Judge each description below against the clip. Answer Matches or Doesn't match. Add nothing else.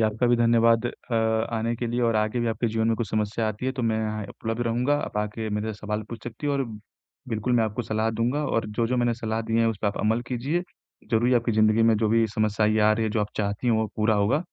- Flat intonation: Matches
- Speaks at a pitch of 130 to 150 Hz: Doesn't match